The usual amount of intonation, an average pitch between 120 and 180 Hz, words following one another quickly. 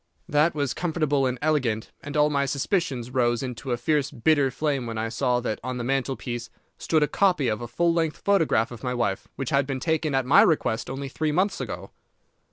Yes: average, 4.0 semitones; low, 135 Hz; fast, 210 wpm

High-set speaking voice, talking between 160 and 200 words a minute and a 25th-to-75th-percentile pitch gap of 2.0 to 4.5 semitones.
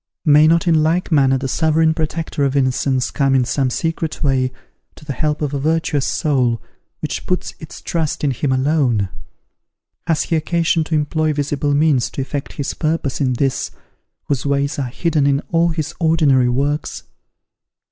No: medium, 145 Hz; average, 170 wpm; average, 2.9 semitones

